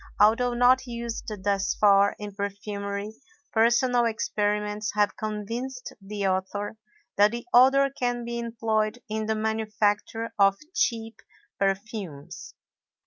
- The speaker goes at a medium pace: No, slow, 115 wpm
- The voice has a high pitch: Yes, high, 215 Hz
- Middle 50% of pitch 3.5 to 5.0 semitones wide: No, narrow, 2.5 semitones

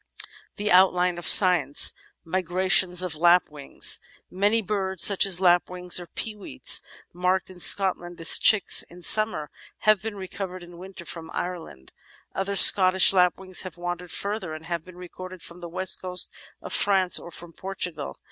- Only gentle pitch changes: Yes, narrow, 1.6 semitones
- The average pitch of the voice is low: No, medium, 180 Hz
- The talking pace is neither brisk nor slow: Yes, average, 155 wpm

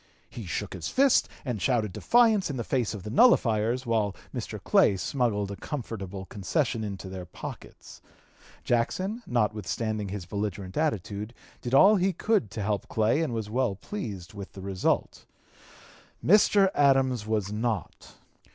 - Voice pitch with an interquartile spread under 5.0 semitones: No, average, 5.3 semitones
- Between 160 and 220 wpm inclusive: No, average, 150 wpm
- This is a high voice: No, low, 110 Hz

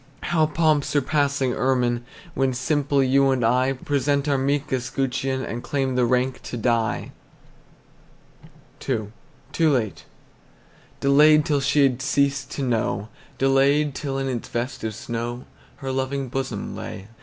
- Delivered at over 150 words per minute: No, average, 140 wpm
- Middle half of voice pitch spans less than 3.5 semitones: Yes, narrow, 2.4 semitones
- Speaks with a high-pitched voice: No, low, 135 Hz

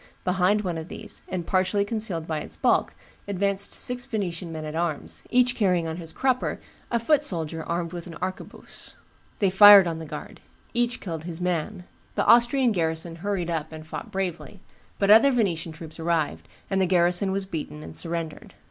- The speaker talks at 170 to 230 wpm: Yes, average, 185 wpm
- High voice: No, medium, 180 Hz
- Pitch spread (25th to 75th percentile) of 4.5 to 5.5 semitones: No, average, 3.8 semitones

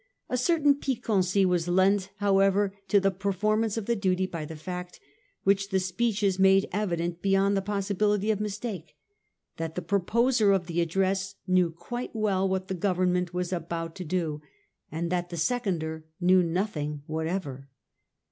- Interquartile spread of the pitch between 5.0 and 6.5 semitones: No, average, 2.7 semitones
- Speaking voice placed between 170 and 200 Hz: Yes, high, 190 Hz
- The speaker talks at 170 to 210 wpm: No, average, 160 wpm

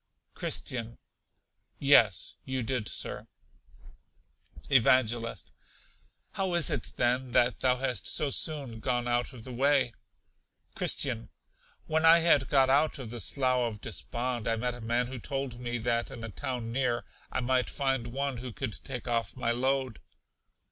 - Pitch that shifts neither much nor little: No, narrow, 2.2 semitones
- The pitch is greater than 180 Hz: No, low, 125 Hz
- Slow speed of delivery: No, average, 155 wpm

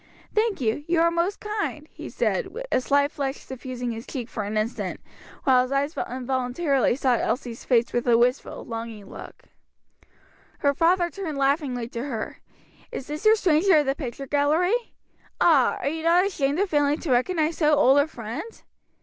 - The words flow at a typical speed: Yes, average, 175 wpm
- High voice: Yes, very high, 285 Hz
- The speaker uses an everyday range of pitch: Yes, average, 5.0 semitones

